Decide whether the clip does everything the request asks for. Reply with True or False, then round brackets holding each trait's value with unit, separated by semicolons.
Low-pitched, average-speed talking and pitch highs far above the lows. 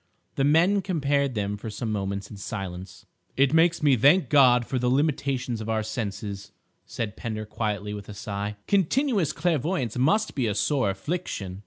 True (120 Hz; 170 wpm; 6.4 semitones)